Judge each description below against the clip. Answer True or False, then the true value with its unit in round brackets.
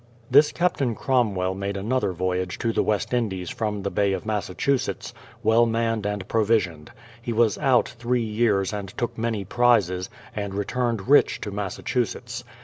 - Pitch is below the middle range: True (110 Hz)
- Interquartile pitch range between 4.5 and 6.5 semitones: False (3.4 semitones)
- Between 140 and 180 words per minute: True (155 wpm)